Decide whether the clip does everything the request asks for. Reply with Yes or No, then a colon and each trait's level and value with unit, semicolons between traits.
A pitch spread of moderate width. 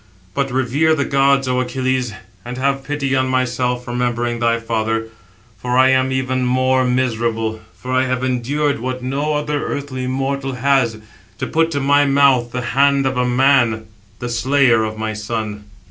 No: narrow, 2.2 semitones